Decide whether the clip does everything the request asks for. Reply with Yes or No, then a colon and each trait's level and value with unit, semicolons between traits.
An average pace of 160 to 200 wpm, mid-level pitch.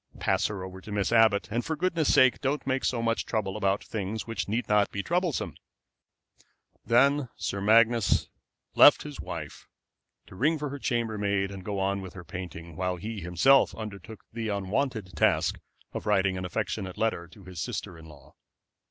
No: average, 180 wpm; low, 105 Hz